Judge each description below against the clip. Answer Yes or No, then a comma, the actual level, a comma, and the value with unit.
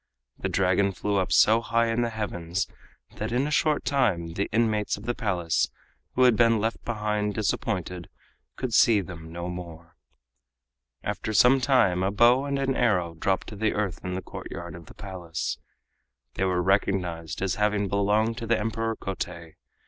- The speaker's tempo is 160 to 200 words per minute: Yes, average, 175 wpm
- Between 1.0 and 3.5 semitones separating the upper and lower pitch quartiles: No, average, 4.1 semitones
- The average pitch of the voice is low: Yes, low, 105 Hz